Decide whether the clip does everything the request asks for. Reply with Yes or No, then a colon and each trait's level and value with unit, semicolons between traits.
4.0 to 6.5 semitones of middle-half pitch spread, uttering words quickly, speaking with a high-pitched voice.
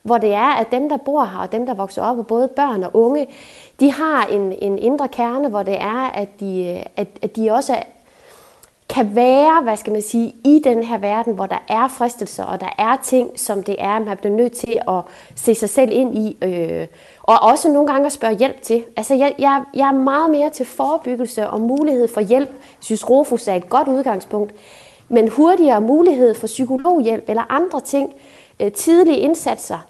No: average, 4.3 semitones; average, 205 wpm; high, 245 Hz